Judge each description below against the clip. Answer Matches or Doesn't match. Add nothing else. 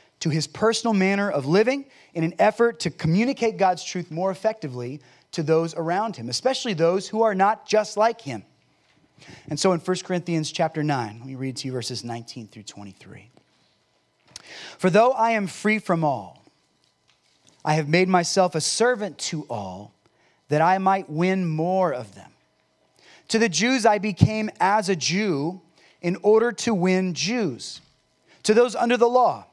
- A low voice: Doesn't match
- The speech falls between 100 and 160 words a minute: Doesn't match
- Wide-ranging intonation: Matches